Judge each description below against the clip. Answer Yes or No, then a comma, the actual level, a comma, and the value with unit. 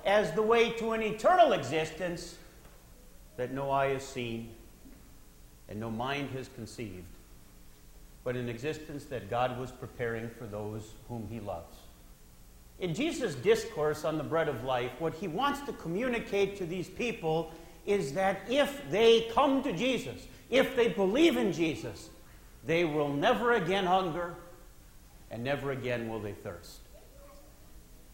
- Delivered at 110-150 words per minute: Yes, average, 145 wpm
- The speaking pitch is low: No, medium, 150 Hz